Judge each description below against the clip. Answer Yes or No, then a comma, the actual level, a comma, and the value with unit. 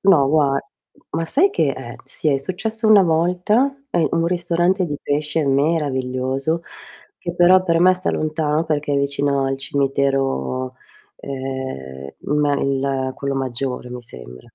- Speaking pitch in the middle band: Yes, medium, 145 Hz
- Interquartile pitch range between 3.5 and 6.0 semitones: Yes, average, 4.2 semitones